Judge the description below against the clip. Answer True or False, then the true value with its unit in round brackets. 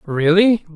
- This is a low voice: False (180 Hz)